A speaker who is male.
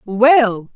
No: female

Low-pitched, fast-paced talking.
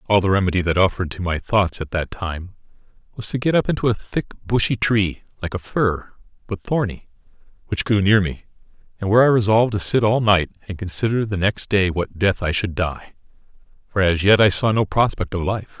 Yes: low, 100 Hz; fast, 215 wpm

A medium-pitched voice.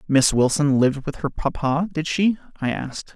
Yes: medium, 145 Hz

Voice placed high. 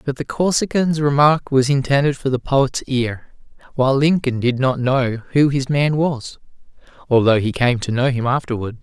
No: low, 135 Hz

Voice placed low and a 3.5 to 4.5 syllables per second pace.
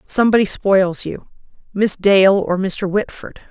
No: high, 195 Hz; 4.2 syllables/s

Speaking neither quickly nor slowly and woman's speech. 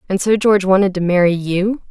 No: fast, 220 wpm; female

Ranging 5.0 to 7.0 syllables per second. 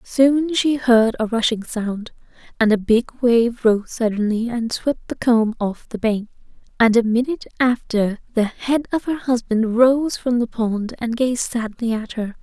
No: 4.1 syllables/s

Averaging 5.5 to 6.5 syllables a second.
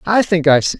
Yes: 6.0 syllables/s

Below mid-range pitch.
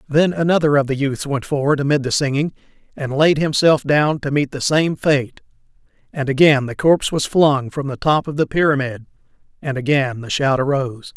No: medium, 145 Hz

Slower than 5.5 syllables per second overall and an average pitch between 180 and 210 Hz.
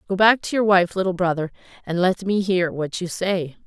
Yes: 5.2 syllables/s; medium, 185 Hz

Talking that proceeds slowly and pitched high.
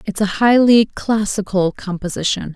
Yes: slow, 120 wpm; high, 205 Hz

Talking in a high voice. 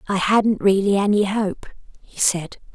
Yes: high, 200 Hz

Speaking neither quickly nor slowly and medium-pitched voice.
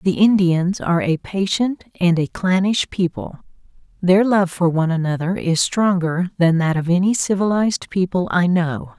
Yes: average, 160 wpm; medium, 180 Hz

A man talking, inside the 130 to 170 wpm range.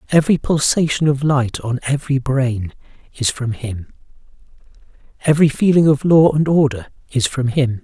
Yes: male; average, 145 wpm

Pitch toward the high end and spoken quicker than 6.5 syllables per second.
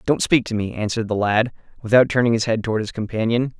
No: low, 115 Hz; 6.7 syllables/s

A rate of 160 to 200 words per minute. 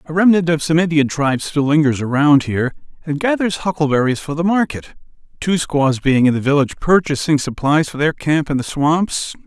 Yes: average, 190 wpm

